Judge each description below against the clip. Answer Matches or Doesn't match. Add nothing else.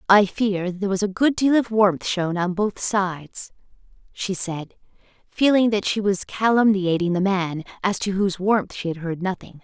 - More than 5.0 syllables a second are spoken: Doesn't match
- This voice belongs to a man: Doesn't match